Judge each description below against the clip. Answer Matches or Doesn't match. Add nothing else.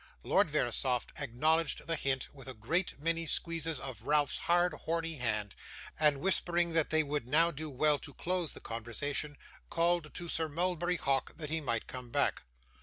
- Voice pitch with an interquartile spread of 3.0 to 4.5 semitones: Matches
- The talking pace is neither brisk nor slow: Matches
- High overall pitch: Doesn't match